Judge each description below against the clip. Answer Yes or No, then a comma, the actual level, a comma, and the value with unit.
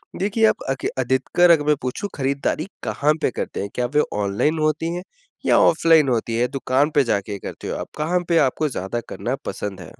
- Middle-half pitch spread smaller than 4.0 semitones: No, average, 4.7 semitones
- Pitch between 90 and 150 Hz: Yes, medium, 140 Hz